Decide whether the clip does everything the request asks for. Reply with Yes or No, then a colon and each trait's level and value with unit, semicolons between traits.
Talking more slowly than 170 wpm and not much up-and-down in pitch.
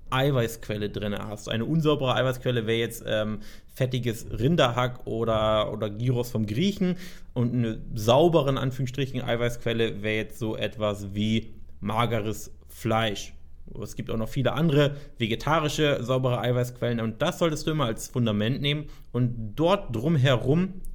No: average, 140 wpm; average, 4.3 semitones